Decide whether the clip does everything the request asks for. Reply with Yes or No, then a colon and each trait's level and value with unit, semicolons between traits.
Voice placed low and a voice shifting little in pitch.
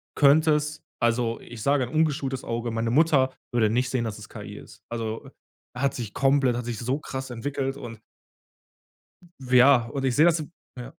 No: low, 130 Hz; average, 3.1 semitones